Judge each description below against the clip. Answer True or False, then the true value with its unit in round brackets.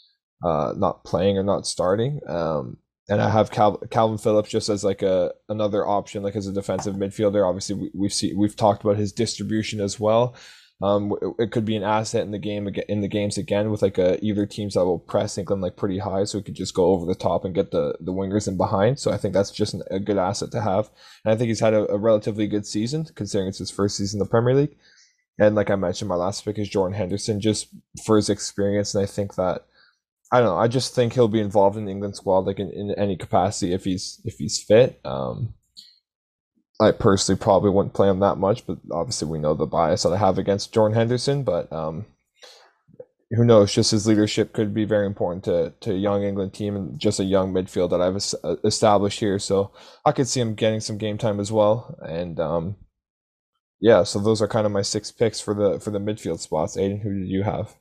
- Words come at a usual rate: False (235 wpm)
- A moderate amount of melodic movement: False (1.8 semitones)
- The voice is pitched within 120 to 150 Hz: False (105 Hz)